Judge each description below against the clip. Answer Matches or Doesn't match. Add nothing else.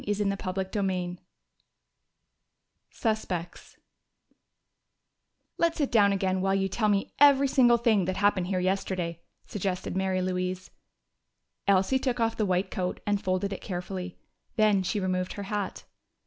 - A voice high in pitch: Matches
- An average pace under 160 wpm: Matches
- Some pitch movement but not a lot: Doesn't match